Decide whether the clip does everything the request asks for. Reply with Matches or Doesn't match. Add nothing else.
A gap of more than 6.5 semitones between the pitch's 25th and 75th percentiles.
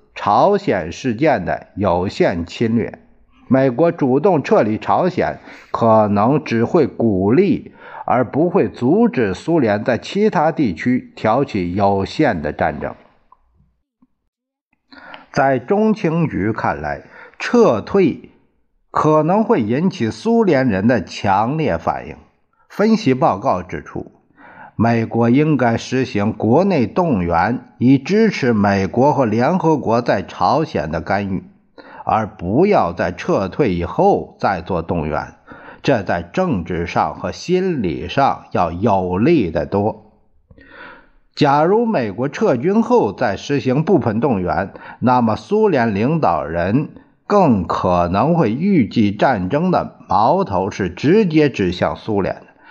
Matches